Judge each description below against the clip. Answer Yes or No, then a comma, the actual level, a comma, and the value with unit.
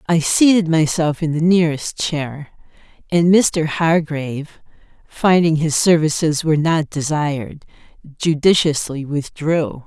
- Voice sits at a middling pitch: Yes, medium, 155 Hz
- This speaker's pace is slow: Yes, slow, 110 wpm